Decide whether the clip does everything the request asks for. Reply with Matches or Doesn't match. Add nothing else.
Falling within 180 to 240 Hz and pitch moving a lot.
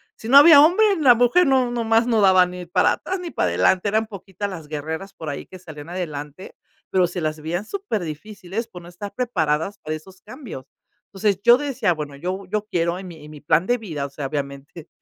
Matches